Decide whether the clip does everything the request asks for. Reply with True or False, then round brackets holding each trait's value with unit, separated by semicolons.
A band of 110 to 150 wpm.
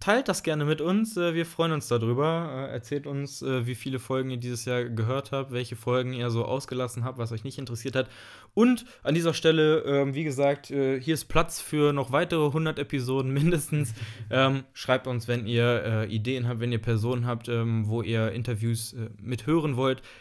False (180 wpm)